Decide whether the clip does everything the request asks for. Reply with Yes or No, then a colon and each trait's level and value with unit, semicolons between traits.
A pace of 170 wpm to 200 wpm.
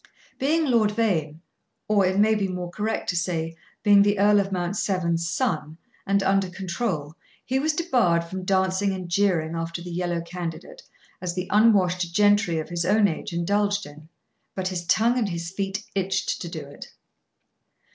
Yes: average, 175 wpm